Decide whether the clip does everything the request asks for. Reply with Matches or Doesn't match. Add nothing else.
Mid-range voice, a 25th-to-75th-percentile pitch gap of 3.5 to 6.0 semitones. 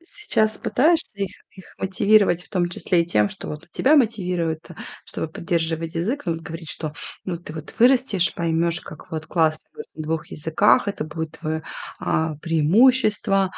Matches